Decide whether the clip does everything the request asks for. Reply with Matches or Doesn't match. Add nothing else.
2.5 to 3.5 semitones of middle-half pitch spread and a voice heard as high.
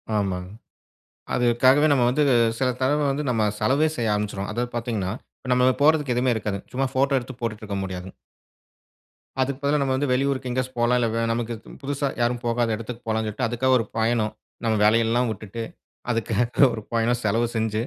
Doesn't match